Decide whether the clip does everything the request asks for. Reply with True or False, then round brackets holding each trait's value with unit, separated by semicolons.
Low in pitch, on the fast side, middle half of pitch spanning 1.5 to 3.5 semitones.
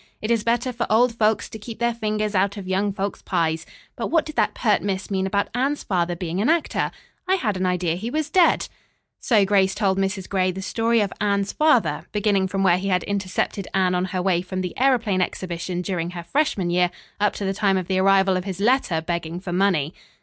False (195 Hz; 225 wpm; 2.9 semitones)